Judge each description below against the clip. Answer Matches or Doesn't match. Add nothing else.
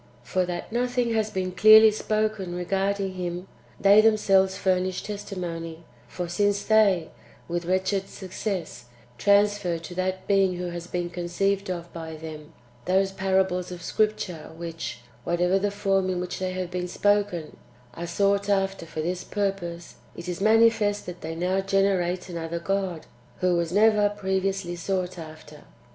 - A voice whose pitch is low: Doesn't match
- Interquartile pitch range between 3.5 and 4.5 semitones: Doesn't match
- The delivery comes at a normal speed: Matches